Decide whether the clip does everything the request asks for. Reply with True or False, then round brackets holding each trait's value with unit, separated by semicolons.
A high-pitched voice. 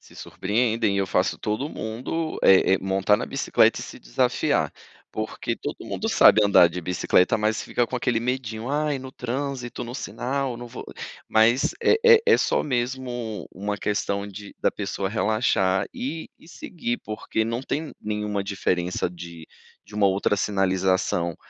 False (110 Hz)